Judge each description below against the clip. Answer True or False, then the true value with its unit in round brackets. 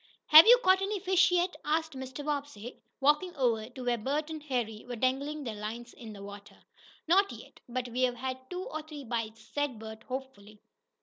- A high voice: True (260 Hz)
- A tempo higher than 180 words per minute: True (190 wpm)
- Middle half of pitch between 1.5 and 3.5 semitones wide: False (4.9 semitones)